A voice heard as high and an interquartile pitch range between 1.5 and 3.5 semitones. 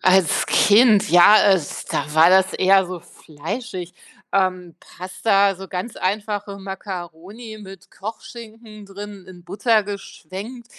Yes: high, 195 Hz; narrow, 2.5 semitones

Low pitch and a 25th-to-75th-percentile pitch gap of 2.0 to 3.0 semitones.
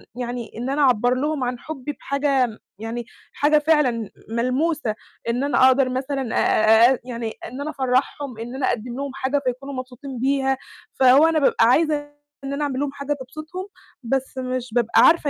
No: very high, 260 Hz; narrow, 2.6 semitones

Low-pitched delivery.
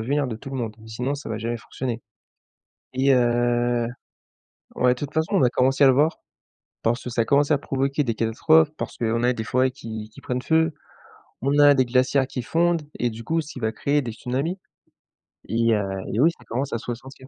Yes: low, 125 Hz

